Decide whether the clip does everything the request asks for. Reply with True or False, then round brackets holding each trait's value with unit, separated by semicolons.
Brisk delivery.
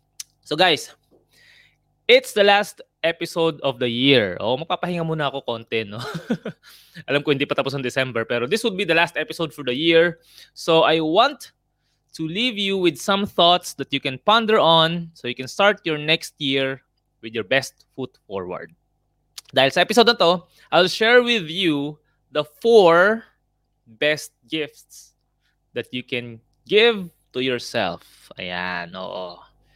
True (160 wpm)